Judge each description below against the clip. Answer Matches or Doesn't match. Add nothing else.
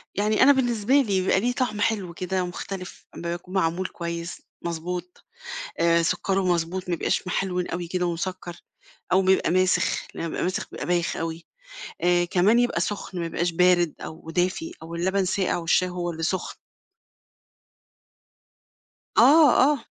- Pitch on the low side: Doesn't match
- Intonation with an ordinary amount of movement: Doesn't match